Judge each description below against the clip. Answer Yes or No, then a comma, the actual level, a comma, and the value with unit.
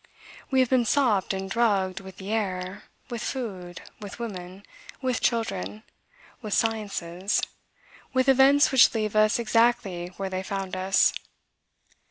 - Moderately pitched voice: No, high, 210 Hz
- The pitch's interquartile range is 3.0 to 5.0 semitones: Yes, average, 3.9 semitones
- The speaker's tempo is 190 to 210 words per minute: No, slow, 135 wpm